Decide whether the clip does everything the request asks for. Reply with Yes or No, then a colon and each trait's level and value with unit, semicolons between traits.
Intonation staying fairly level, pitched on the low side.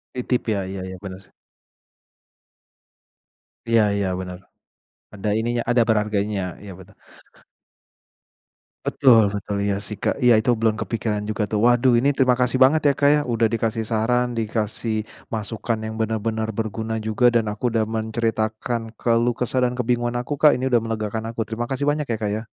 Yes: narrow, 2.1 semitones; low, 115 Hz